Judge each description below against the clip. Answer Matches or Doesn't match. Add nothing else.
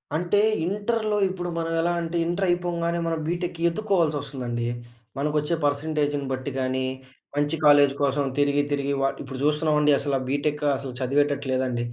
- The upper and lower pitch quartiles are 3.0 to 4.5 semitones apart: Matches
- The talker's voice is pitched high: Doesn't match